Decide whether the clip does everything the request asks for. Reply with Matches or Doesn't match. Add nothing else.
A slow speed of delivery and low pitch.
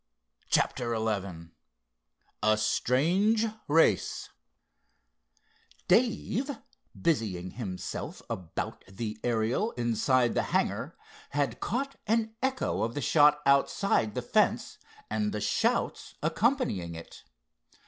Matches